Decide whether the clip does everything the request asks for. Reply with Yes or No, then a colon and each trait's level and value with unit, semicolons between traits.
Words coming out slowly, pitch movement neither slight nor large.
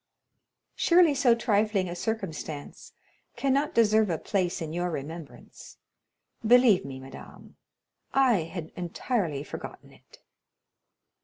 No: slow, 105 wpm; wide, 6.4 semitones